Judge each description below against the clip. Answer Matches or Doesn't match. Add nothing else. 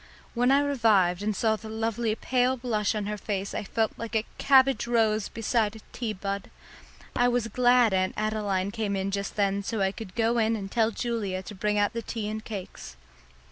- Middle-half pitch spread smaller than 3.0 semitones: Matches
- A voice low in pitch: Doesn't match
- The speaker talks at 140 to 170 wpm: Doesn't match